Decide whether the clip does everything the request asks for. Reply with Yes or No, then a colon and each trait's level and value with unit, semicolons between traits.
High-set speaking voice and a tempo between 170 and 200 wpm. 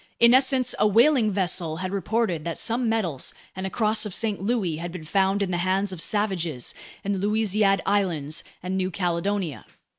Yes: high, 195 Hz; average, 185 wpm